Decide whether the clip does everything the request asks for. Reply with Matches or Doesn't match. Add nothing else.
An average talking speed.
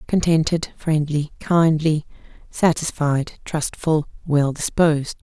Doesn't match